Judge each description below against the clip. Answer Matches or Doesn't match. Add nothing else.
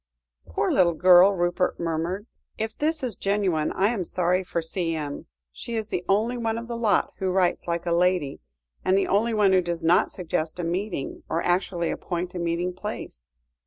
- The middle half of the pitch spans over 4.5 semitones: Doesn't match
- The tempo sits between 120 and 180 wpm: Doesn't match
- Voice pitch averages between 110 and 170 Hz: Doesn't match